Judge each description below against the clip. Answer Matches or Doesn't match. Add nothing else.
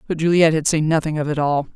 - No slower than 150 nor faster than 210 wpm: Doesn't match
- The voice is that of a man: Doesn't match